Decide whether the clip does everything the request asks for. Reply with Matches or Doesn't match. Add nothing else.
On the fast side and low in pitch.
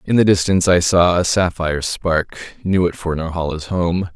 Doesn't match